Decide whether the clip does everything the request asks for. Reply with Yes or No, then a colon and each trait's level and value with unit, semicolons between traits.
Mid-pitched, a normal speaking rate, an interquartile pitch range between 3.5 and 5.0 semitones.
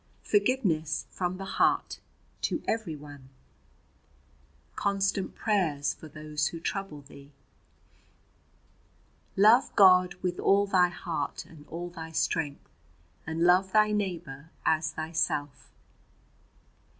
No: medium, 170 Hz; slow, 100 wpm; average, 4.2 semitones